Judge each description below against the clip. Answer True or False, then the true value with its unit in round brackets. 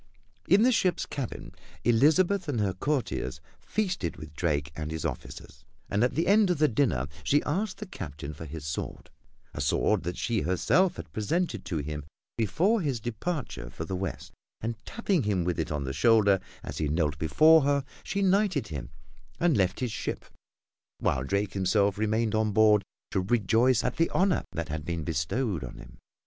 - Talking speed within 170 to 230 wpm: True (185 wpm)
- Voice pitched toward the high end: False (110 Hz)